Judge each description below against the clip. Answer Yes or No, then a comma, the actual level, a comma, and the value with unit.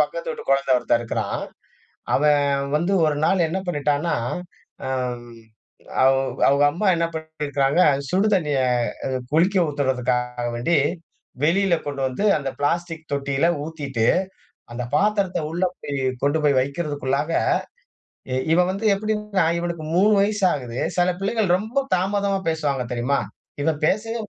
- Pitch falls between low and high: Yes, medium, 155 Hz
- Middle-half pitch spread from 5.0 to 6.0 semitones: Yes, wide, 5.5 semitones